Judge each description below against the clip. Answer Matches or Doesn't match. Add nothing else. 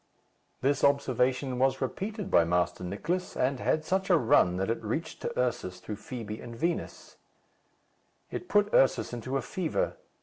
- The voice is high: Doesn't match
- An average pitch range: Doesn't match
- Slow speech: Doesn't match